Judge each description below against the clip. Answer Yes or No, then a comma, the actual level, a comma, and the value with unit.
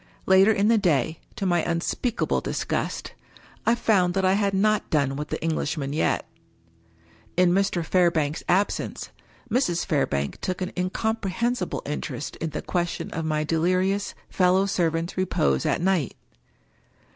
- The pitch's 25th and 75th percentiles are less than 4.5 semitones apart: Yes, average, 3.6 semitones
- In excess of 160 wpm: No, average, 145 wpm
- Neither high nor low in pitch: Yes, medium, 180 Hz